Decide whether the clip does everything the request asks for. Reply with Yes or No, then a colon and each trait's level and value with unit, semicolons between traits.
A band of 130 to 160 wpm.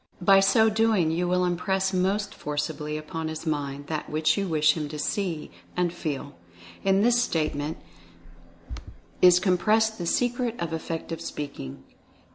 Yes: average, 145 wpm